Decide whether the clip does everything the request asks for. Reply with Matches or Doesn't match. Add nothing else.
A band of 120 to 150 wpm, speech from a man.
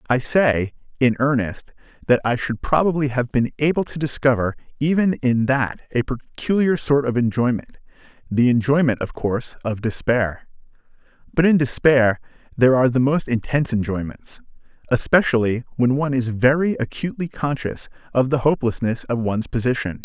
Matches